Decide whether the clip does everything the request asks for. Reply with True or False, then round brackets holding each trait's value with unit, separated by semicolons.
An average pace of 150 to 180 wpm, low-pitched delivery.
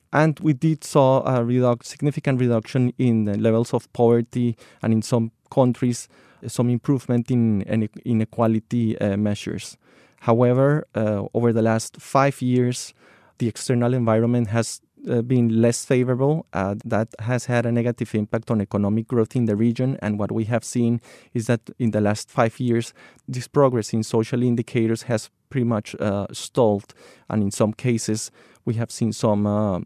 True (165 wpm; 120 Hz)